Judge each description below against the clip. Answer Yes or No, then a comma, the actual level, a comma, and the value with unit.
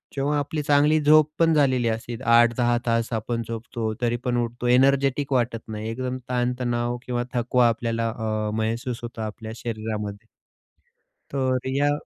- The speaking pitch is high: No, low, 120 Hz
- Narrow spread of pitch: Yes, narrow, 2.3 semitones